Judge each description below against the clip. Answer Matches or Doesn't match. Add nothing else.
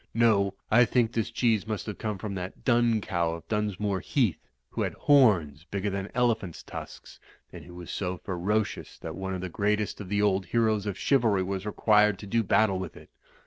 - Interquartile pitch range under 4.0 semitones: Matches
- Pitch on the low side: Matches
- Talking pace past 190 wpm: Matches